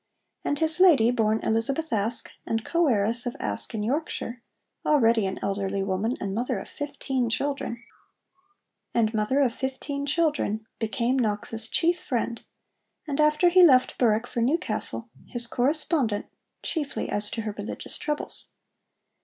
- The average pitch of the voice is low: No, high, 240 Hz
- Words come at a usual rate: No, slow, 130 wpm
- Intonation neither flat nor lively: Yes, average, 4.7 semitones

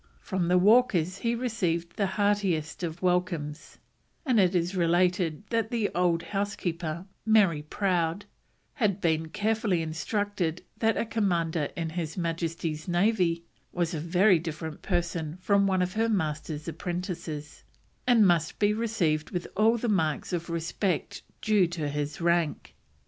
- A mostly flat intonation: No, average, 3.7 semitones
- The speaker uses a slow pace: No, average, 145 wpm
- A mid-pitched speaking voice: Yes, medium, 175 Hz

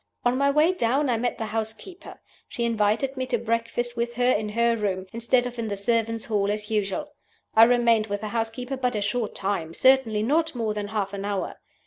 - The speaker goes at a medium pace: No, fast, 210 wpm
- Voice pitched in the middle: No, high, 230 Hz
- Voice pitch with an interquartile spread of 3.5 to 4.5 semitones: No, average, 2.8 semitones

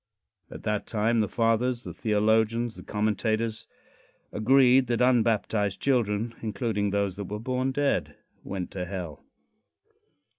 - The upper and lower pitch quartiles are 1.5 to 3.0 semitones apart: Yes, average, 2.7 semitones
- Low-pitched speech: Yes, low, 110 Hz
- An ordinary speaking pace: No, slow, 125 wpm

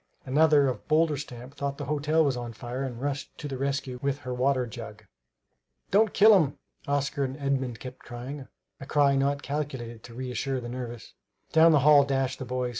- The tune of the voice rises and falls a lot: No, narrow, 2.4 semitones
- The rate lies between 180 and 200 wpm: Yes, average, 190 wpm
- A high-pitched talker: No, low, 135 Hz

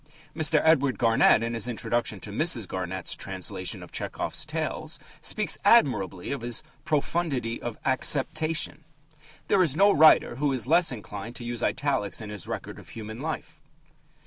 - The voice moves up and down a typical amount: No, wide, 5.7 semitones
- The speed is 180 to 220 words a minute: No, average, 155 wpm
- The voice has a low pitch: Yes, low, 125 Hz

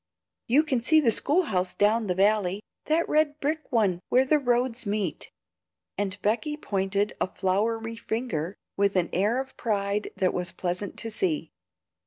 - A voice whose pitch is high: Yes, high, 215 Hz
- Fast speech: No, average, 165 wpm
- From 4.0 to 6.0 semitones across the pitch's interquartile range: Yes, average, 5.0 semitones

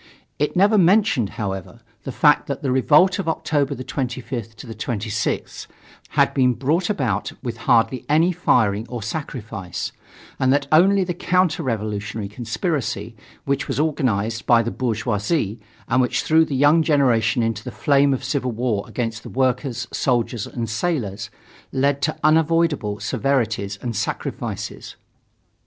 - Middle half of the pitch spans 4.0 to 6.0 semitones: Yes, average, 4.9 semitones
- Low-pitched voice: Yes, low, 130 Hz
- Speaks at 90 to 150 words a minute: Yes, average, 140 wpm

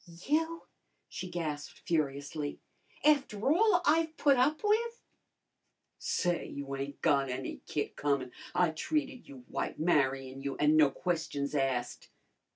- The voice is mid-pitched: Yes, medium, 155 Hz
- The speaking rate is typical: No, slow, 130 wpm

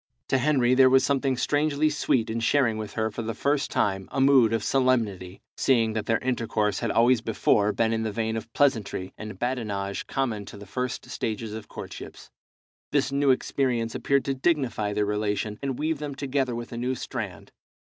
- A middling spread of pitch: Yes, average, 3.8 semitones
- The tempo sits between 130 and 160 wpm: No, average, 190 wpm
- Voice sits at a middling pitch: No, low, 120 Hz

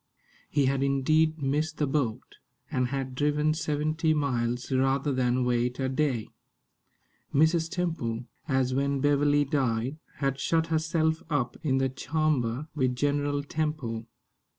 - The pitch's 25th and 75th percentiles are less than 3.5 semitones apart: Yes, average, 3.1 semitones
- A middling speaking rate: No, slow, 130 wpm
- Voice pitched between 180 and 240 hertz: No, medium, 140 Hz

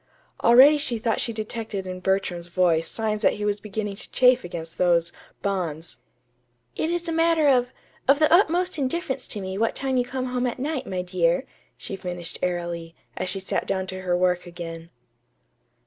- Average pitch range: No, wide, 6.3 semitones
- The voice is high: Yes, high, 205 Hz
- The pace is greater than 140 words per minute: Yes, average, 185 wpm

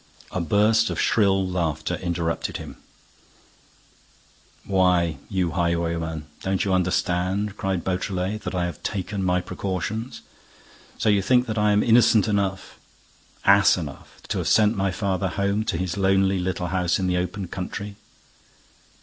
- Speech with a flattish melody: Yes, narrow, 2.2 semitones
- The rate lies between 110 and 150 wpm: Yes, average, 145 wpm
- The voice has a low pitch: Yes, very low, 95 Hz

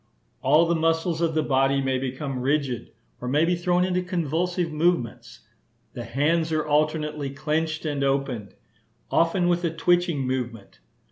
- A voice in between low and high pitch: Yes, medium, 155 Hz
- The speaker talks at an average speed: Yes, average, 150 wpm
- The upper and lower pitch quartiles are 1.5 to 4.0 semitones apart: Yes, average, 3.6 semitones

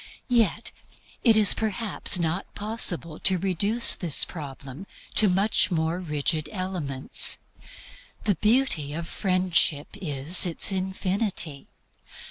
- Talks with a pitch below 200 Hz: Yes, medium, 185 Hz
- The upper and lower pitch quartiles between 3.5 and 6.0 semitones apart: Yes, average, 4.2 semitones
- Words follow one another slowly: Yes, slow, 105 wpm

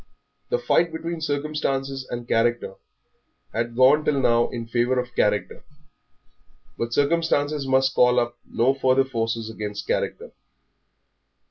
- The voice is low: Yes, low, 130 Hz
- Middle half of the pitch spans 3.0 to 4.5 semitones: Yes, average, 3.4 semitones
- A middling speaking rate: No, slow, 125 wpm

